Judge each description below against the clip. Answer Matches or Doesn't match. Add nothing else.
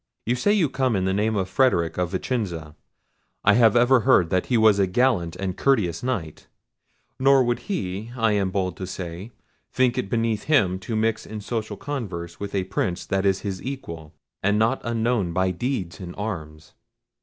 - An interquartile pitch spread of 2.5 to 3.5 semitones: Doesn't match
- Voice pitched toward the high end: Doesn't match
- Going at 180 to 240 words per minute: Matches